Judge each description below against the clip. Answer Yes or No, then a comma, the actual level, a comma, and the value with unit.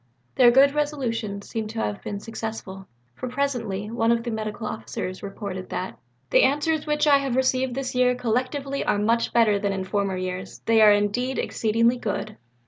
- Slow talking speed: No, average, 180 wpm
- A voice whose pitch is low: No, high, 230 Hz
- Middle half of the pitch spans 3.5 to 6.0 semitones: Yes, average, 3.9 semitones